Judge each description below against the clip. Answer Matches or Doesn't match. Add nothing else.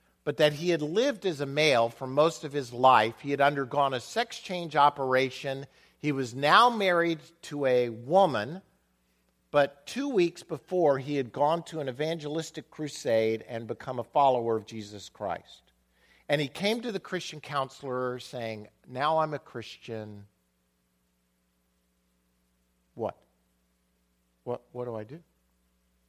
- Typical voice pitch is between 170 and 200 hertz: Doesn't match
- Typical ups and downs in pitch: Doesn't match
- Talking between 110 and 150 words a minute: Matches